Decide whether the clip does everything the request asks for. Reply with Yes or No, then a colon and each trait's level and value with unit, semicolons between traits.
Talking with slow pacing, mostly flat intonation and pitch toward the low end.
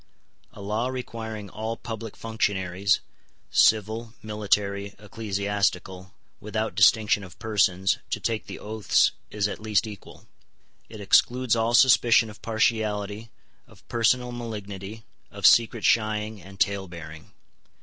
Yes: slow, 120 wpm; narrow, 2.1 semitones; low, 105 Hz